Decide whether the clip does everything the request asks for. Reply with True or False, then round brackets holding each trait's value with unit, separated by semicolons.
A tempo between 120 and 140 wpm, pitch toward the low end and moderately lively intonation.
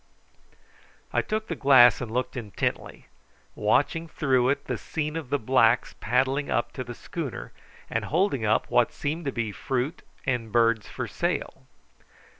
False (155 wpm; 130 Hz; 3.9 semitones)